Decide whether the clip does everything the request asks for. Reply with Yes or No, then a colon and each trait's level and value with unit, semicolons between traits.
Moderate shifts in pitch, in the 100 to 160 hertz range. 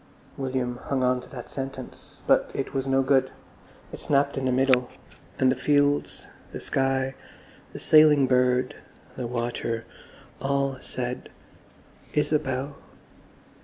No: narrow, 1.5 semitones; low, 135 Hz